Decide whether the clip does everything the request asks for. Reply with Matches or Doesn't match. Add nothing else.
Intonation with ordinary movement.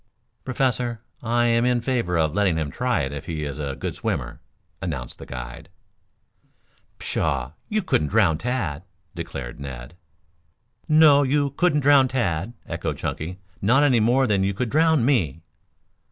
Doesn't match